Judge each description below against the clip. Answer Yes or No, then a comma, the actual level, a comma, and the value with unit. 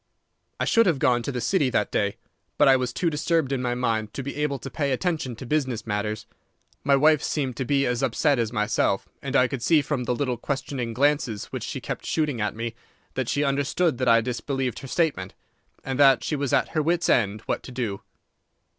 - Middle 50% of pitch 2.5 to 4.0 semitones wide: Yes, average, 3.4 semitones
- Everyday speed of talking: No, fast, 220 wpm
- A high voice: No, low, 130 Hz